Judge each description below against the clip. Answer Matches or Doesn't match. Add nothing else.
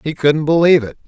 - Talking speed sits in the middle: Doesn't match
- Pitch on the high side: Doesn't match